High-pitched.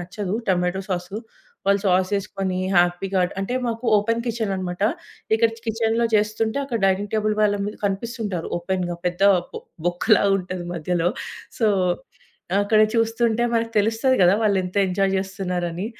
Yes: high, 200 Hz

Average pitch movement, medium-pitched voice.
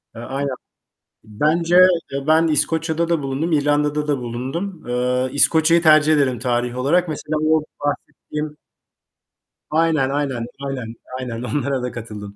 Yes: average, 3.9 semitones; medium, 145 Hz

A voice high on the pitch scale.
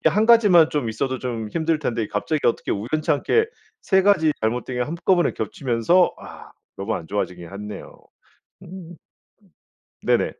No: medium, 140 Hz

